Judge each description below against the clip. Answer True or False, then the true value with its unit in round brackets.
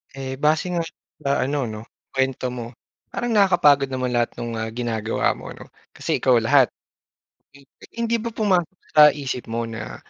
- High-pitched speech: False (135 Hz)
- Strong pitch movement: False (4.6 semitones)